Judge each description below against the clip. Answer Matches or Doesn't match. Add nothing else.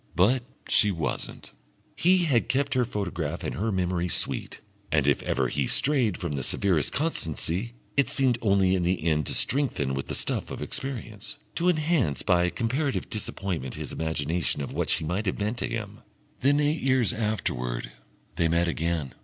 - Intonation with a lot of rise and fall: Matches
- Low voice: Matches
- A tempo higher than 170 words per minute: Matches